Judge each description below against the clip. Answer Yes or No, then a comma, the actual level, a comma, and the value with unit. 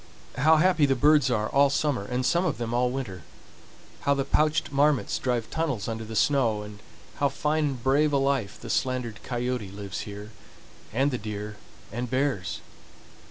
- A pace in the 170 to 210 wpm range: Yes, average, 175 wpm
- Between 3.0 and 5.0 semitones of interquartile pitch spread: Yes, average, 4.4 semitones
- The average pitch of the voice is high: No, low, 130 Hz